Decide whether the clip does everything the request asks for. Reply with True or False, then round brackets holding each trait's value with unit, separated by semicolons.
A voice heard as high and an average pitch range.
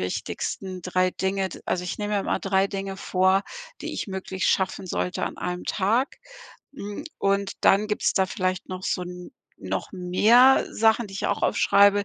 False (195 Hz; 1.6 semitones)